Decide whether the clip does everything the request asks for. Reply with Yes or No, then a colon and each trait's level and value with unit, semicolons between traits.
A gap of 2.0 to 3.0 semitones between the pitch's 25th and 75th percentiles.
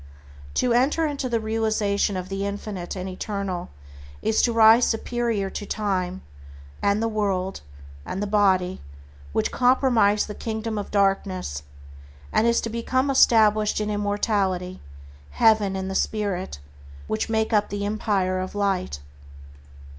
Yes: narrow, 2.5 semitones